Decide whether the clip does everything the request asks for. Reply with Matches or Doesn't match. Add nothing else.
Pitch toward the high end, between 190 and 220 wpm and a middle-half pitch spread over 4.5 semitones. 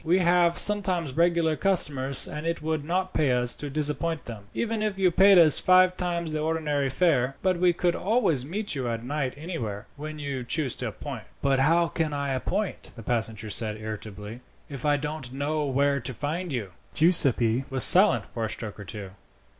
Doesn't match